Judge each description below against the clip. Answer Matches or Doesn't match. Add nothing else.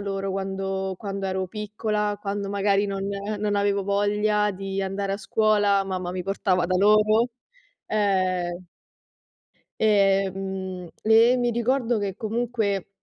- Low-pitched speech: Doesn't match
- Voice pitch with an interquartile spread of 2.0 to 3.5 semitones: Doesn't match